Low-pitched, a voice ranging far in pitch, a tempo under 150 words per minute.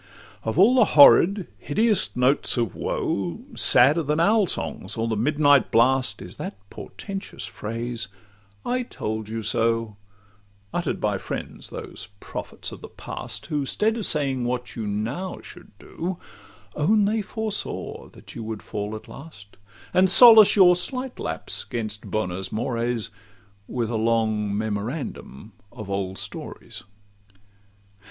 Yes: low, 120 Hz; wide, 8.5 semitones; average, 140 wpm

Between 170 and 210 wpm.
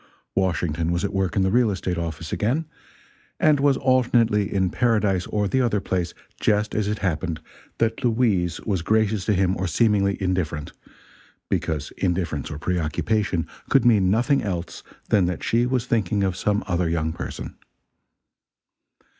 No: average, 155 wpm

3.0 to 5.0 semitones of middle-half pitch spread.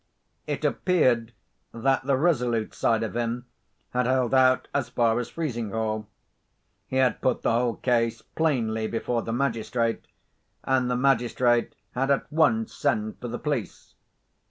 No: narrow, 2.4 semitones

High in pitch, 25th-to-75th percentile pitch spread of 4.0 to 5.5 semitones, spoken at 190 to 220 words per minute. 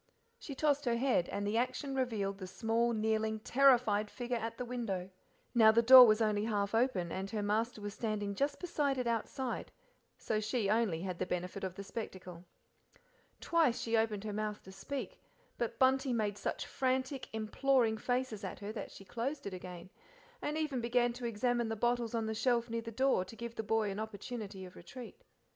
No: high, 225 Hz; average, 3.2 semitones; average, 195 wpm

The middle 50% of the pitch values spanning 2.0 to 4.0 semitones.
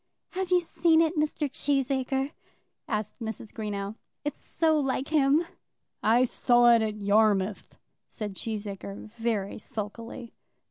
No: average, 5.3 semitones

